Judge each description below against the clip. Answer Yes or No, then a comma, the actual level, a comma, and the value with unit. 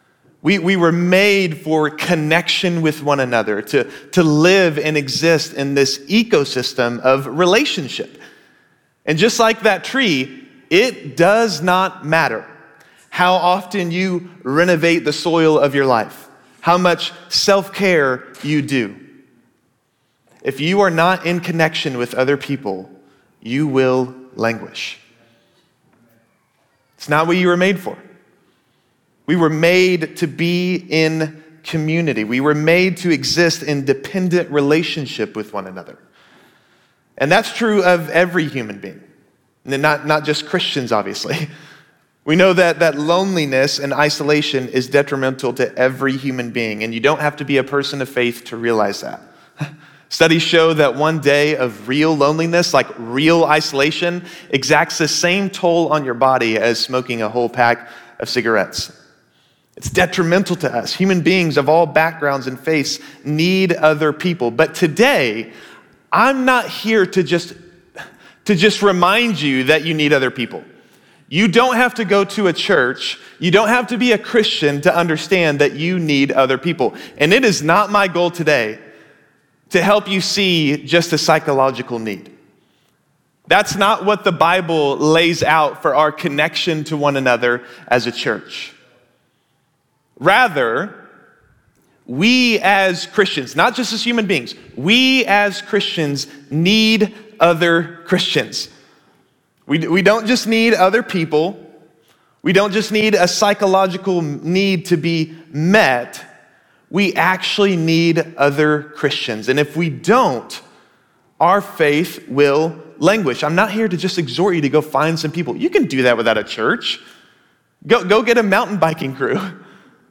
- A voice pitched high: No, medium, 160 Hz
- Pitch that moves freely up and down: No, average, 4.7 semitones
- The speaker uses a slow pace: No, average, 145 wpm